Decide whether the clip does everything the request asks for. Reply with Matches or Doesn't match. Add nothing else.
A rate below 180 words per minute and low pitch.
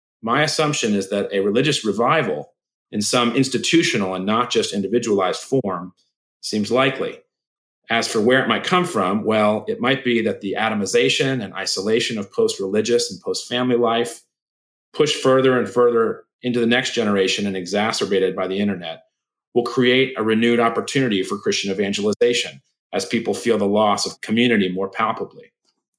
Matches